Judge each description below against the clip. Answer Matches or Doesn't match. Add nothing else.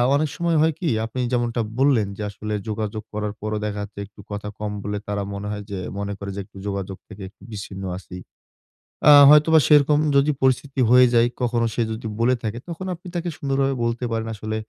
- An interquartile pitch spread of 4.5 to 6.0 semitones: Matches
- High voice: Doesn't match